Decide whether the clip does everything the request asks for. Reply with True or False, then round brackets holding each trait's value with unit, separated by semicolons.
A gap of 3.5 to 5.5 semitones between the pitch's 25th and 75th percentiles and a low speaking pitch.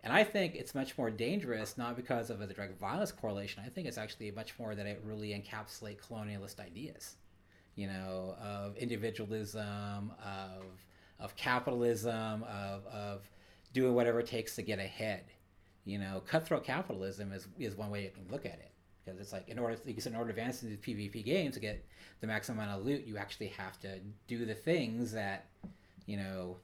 False (3.1 semitones; 105 Hz)